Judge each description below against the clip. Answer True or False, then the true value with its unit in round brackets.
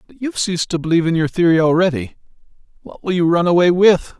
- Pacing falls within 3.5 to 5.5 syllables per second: False (6.9 syllables/s)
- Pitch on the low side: False (175 Hz)